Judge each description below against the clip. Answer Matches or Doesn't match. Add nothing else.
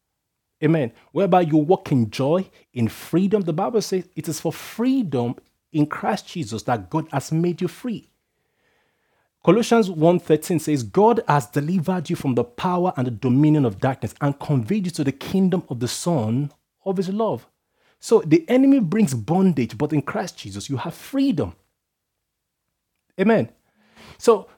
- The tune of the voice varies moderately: Doesn't match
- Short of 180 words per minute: Matches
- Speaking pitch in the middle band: Matches